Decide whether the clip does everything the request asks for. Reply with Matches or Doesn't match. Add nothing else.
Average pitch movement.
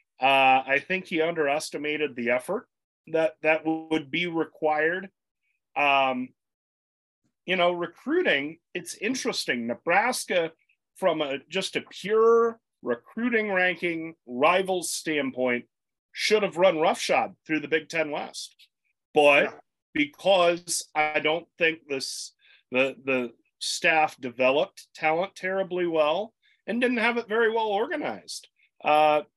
Matches